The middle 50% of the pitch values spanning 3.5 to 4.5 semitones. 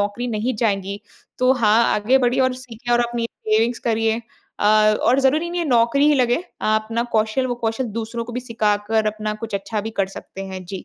No: narrow, 2.6 semitones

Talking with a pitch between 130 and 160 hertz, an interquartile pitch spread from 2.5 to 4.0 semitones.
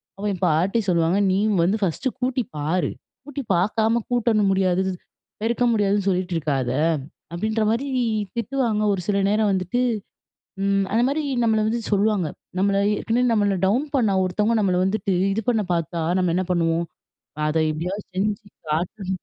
No: high, 200 Hz; average, 3.5 semitones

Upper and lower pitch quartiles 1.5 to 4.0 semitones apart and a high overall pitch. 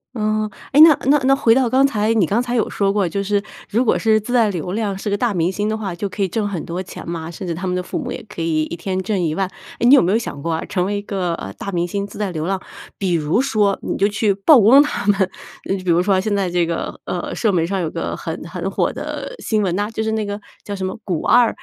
Yes: average, 3.5 semitones; high, 200 Hz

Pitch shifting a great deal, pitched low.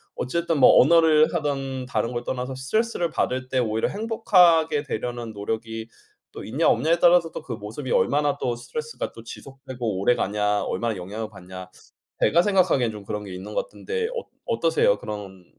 Yes: wide, 7.1 semitones; low, 130 Hz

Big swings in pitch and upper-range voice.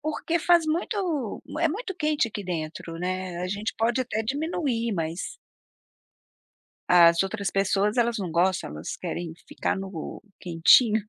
Yes: wide, 8.4 semitones; high, 210 Hz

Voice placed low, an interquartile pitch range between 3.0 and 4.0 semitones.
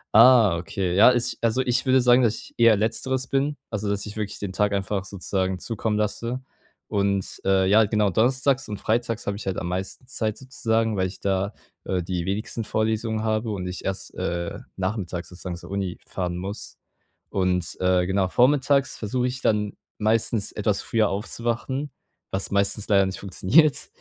Yes: low, 105 Hz; average, 3.5 semitones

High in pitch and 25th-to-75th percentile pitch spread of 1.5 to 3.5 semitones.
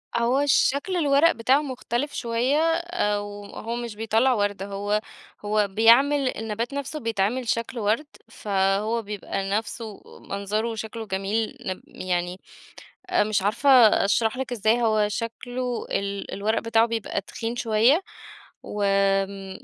Yes: high, 225 Hz; average, 3.1 semitones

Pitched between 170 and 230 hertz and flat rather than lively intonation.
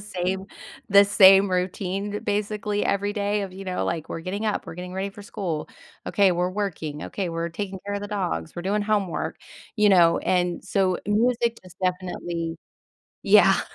Yes: high, 190 Hz; narrow, 2.3 semitones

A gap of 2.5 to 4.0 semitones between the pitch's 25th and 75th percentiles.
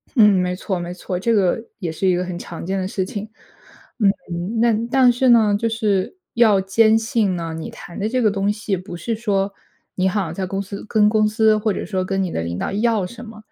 Yes: average, 3.2 semitones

